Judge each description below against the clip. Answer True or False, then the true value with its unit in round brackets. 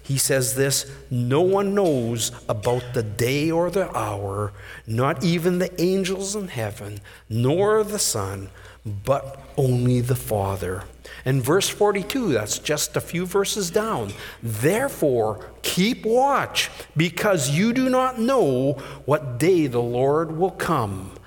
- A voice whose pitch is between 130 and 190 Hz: True (135 Hz)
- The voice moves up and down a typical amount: False (8.5 semitones)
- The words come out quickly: False (135 wpm)